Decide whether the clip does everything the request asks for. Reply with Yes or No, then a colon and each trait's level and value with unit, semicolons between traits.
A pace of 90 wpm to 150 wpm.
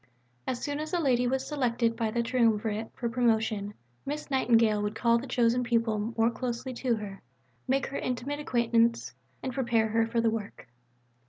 No: average, 175 wpm